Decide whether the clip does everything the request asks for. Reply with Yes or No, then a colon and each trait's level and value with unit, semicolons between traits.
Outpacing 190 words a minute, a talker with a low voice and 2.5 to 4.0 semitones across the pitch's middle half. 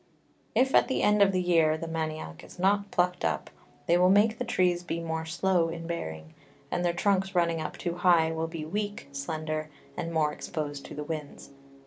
No: average, 200 wpm; medium, 170 Hz; average, 2.8 semitones